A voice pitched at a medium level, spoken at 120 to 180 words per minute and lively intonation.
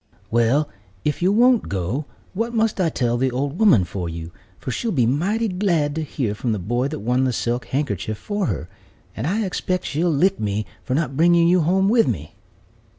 No: medium, 145 Hz; fast, 205 wpm; wide, 7.6 semitones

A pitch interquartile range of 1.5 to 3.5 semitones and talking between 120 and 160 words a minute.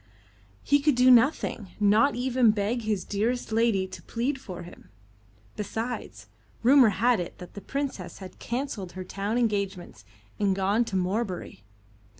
No: average, 4.4 semitones; average, 150 wpm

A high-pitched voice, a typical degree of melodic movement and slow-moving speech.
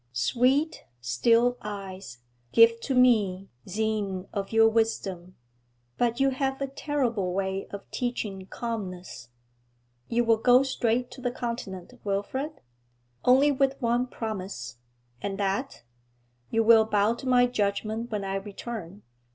Yes: high, 225 Hz; average, 4.1 semitones; slow, 130 wpm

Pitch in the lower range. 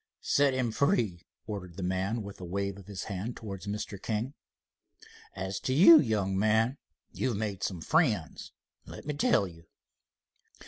Yes: low, 105 Hz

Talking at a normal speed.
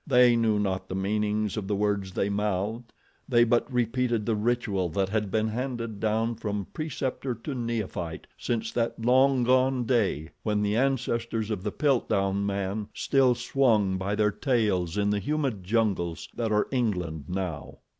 Yes: average, 165 wpm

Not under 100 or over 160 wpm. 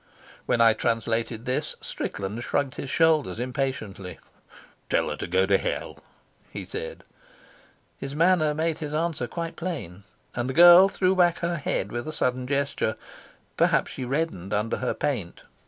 Yes: average, 155 wpm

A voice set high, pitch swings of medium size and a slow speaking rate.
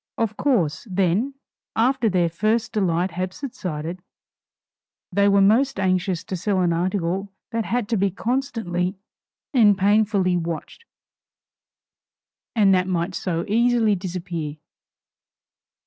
Yes: high, 195 Hz; average, 3.8 semitones; slow, 115 wpm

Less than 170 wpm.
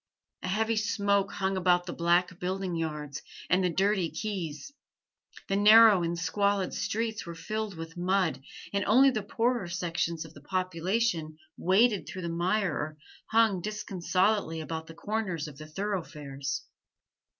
Yes: average, 150 wpm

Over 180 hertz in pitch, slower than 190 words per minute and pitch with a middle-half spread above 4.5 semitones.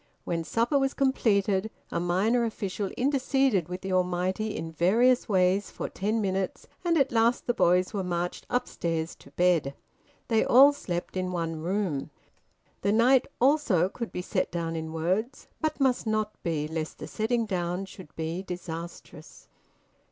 Yes: high, 190 Hz; average, 160 wpm; average, 5.1 semitones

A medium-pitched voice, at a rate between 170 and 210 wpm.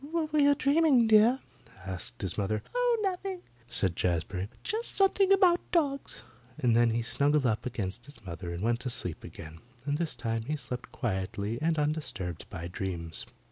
No: low, 125 Hz; average, 175 wpm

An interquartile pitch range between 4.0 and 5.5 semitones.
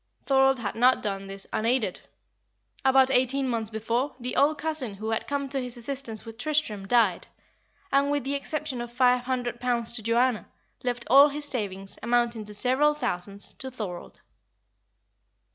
No: average, 3.3 semitones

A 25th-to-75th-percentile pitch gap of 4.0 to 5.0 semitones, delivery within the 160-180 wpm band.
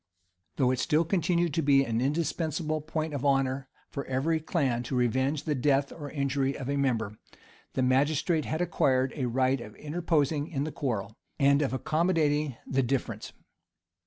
No: average, 3.0 semitones; average, 165 wpm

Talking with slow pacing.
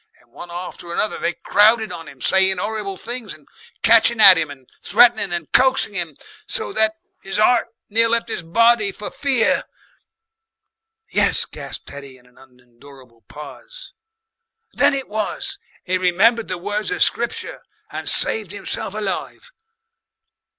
No: average, 145 wpm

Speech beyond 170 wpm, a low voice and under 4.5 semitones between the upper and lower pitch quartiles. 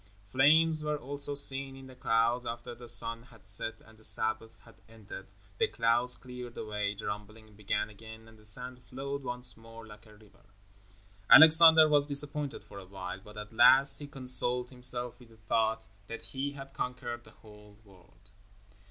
Yes: average, 180 wpm; low, 120 Hz; average, 3.7 semitones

